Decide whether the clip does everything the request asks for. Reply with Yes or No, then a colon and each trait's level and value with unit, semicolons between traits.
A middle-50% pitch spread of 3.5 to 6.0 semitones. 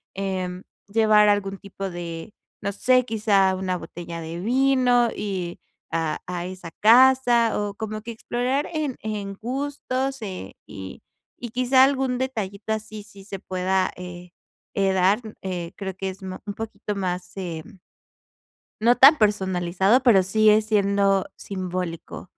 Yes: average, 3.9 semitones